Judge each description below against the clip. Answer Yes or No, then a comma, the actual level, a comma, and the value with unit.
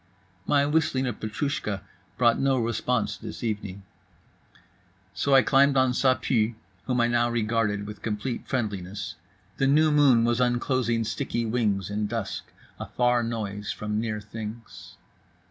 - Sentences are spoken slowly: No, average, 145 wpm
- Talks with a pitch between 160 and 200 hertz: No, low, 115 Hz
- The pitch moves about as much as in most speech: Yes, average, 3.4 semitones